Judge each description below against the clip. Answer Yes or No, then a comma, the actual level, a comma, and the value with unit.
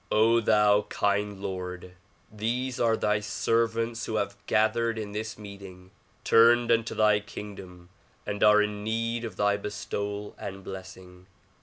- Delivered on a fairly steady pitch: Yes, narrow, 2.1 semitones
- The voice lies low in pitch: Yes, low, 105 Hz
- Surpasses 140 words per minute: No, slow, 135 wpm